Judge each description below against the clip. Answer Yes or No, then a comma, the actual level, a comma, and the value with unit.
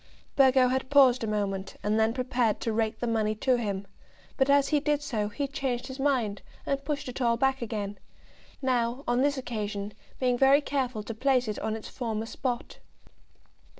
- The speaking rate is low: No, average, 185 wpm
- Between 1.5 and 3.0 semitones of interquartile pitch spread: No, average, 3.6 semitones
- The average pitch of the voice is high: Yes, high, 245 Hz